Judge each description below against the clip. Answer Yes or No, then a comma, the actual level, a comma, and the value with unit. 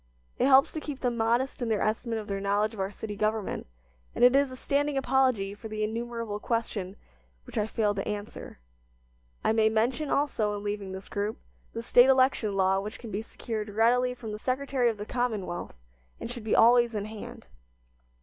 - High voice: Yes, high, 225 Hz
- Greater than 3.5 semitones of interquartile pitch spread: No, average, 3.1 semitones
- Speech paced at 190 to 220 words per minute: Yes, average, 200 wpm